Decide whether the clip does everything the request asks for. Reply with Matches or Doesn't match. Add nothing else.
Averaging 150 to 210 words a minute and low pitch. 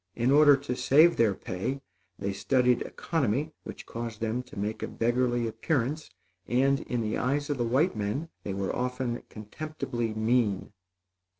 Matches